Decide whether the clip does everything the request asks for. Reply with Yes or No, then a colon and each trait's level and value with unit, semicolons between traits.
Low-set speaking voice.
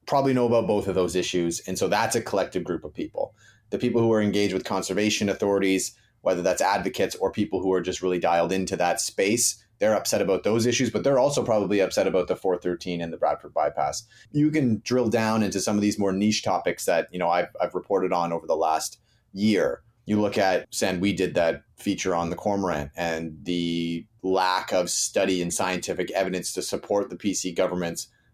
Yes: very low, 95 Hz